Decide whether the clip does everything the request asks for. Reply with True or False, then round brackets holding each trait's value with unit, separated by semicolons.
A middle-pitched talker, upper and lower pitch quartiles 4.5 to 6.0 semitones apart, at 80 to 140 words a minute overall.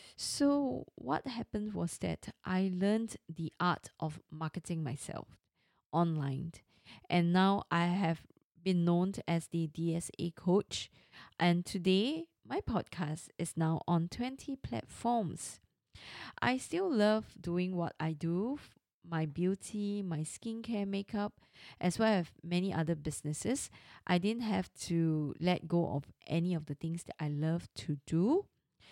False (175 Hz; 3.8 semitones; 135 wpm)